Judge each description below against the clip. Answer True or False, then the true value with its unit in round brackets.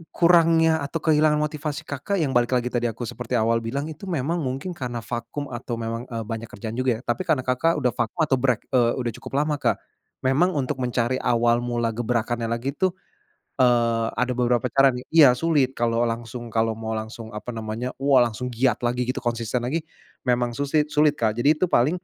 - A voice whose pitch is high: False (125 Hz)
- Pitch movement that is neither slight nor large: True (3.4 semitones)